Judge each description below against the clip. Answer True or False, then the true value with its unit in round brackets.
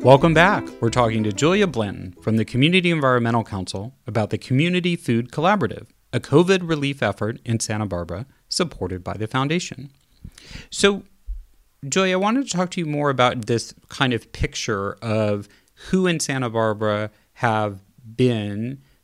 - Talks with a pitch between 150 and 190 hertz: False (120 Hz)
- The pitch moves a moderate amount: False (5.9 semitones)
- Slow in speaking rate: False (155 wpm)